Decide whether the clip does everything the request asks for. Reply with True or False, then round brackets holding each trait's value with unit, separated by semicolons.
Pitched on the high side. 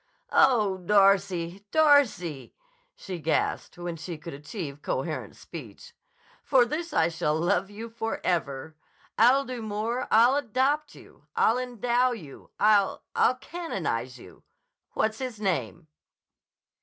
True (210 Hz)